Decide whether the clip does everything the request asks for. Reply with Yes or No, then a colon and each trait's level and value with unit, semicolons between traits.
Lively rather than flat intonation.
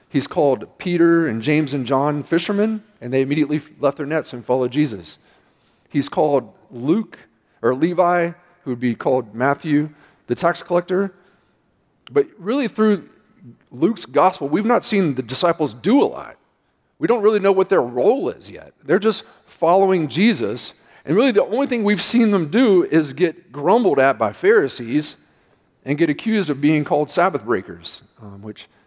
Yes: wide, 6.2 semitones